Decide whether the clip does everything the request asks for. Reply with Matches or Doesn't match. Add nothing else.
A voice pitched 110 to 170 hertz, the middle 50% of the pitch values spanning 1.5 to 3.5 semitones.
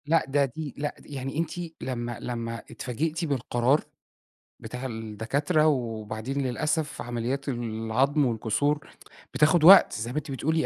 Doesn't match